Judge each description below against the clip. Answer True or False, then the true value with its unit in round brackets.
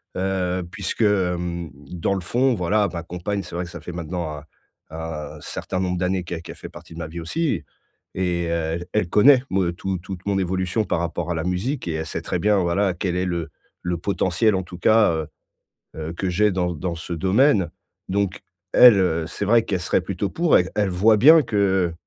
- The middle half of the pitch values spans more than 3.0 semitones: False (2.7 semitones)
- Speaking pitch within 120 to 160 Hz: False (90 Hz)